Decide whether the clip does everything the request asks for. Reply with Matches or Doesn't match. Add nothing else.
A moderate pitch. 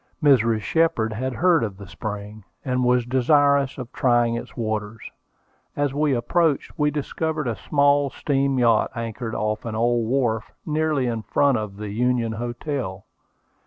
Doesn't match